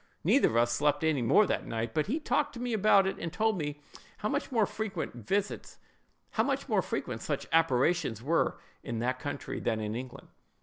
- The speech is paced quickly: No, average, 175 wpm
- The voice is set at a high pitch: No, medium, 155 Hz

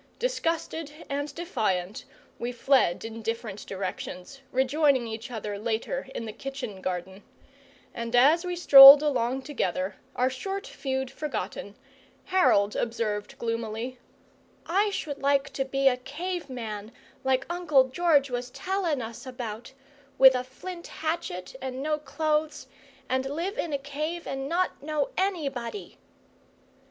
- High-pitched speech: Yes, very high, 265 Hz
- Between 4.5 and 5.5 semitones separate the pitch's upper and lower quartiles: Yes, average, 5.1 semitones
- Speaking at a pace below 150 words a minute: Yes, slow, 135 wpm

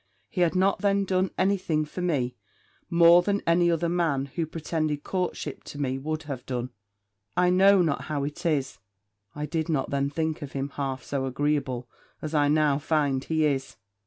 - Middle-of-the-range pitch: Yes, medium, 155 Hz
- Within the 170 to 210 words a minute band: Yes, average, 185 wpm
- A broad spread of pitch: No, average, 3.8 semitones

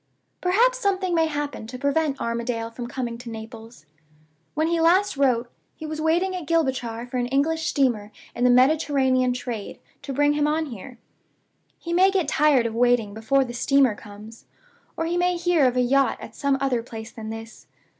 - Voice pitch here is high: Yes, very high, 270 Hz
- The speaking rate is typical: Yes, average, 185 wpm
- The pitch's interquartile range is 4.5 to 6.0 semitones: Yes, average, 5.3 semitones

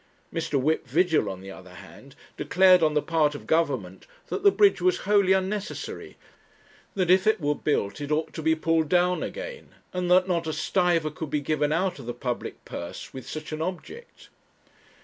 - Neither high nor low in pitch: Yes, medium, 160 Hz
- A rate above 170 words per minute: Yes, average, 190 wpm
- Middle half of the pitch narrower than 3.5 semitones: No, average, 3.9 semitones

